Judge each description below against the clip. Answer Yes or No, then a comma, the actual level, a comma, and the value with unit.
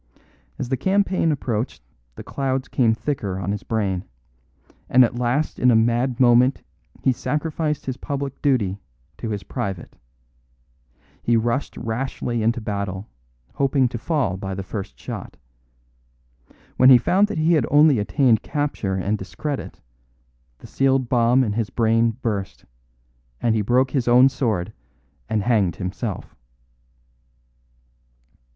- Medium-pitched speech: No, low, 120 Hz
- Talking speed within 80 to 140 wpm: Yes, slow, 135 wpm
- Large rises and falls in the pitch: No, average, 4.3 semitones